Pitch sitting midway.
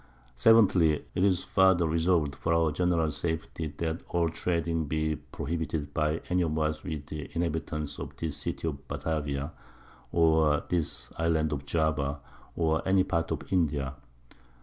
No: very low, 80 Hz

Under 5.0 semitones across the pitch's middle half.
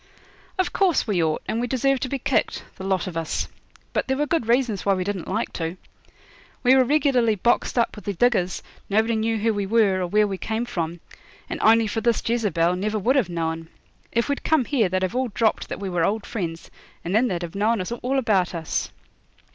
Yes: average, 4.6 semitones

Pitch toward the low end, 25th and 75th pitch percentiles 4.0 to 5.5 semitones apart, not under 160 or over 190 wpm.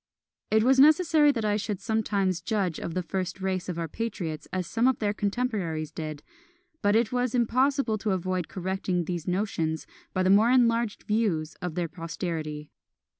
No: high, 195 Hz; average, 4.8 semitones; average, 175 wpm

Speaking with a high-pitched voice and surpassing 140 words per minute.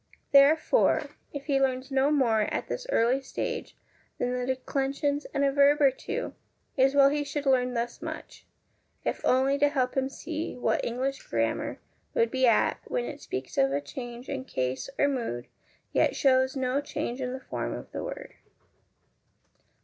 Yes: very high, 265 Hz; average, 180 wpm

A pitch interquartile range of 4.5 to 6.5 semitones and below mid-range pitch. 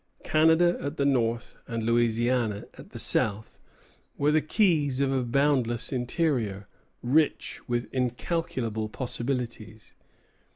No: average, 3.7 semitones; low, 125 Hz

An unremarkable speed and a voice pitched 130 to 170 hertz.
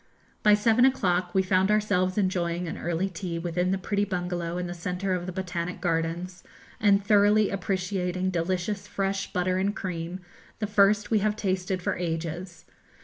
No: average, 165 wpm; medium, 185 Hz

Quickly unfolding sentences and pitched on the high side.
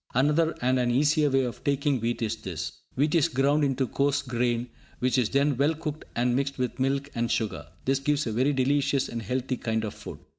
No: fast, 215 wpm; low, 130 Hz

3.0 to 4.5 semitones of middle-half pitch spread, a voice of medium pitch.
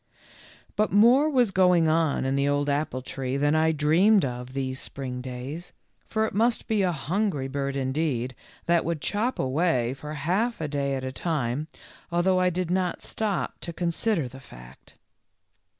No: wide, 5.5 semitones; medium, 155 Hz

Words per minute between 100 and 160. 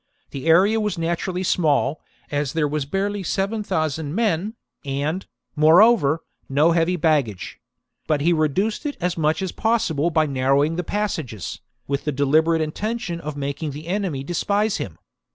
Yes: average, 155 wpm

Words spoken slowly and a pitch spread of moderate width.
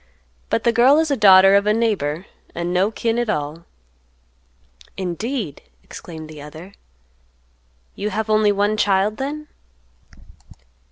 Yes: slow, 130 wpm; average, 4.4 semitones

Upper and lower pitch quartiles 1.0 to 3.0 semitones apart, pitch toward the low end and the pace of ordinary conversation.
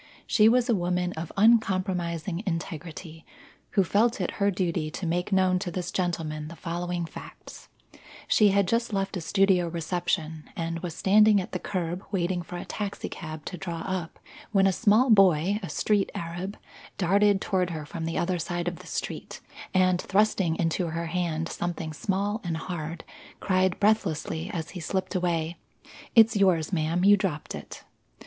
No: average, 2.7 semitones; medium, 180 Hz; average, 170 wpm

